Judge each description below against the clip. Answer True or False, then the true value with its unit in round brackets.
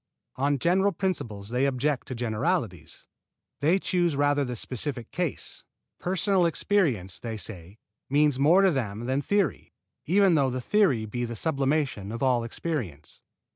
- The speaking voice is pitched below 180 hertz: True (135 Hz)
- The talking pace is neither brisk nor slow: True (145 wpm)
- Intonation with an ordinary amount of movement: False (6.4 semitones)